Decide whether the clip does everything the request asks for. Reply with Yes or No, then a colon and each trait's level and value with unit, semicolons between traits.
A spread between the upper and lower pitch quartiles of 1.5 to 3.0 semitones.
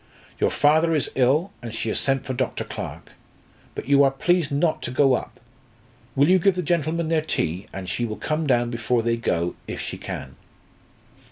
No: average, 4.9 semitones